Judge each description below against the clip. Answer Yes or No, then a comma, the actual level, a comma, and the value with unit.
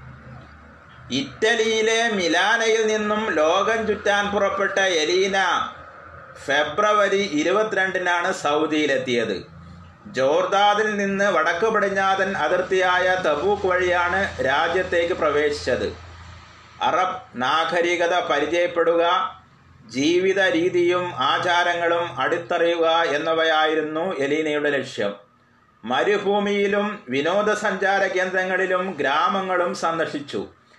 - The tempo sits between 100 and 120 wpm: No, average, 65 wpm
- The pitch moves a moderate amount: Yes, average, 3.4 semitones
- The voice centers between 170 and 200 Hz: Yes, medium, 185 Hz